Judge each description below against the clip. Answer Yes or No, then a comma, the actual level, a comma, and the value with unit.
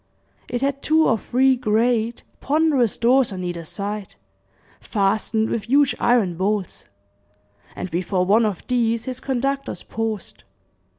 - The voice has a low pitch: No, high, 225 Hz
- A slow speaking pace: Yes, slow, 130 wpm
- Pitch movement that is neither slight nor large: Yes, average, 4.2 semitones